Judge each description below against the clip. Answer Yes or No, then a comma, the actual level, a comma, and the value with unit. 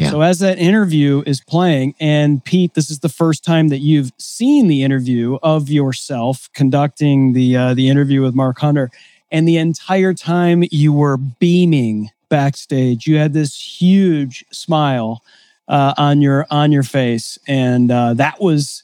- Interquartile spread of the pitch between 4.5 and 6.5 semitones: No, average, 3.4 semitones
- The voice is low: No, medium, 145 Hz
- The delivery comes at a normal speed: Yes, average, 160 wpm